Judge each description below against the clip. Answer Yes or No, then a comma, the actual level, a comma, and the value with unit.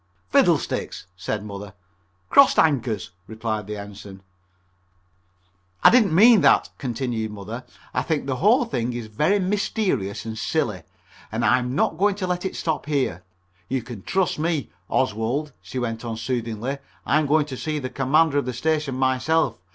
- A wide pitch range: Yes, wide, 6.1 semitones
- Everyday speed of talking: Yes, average, 160 wpm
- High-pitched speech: No, low, 130 Hz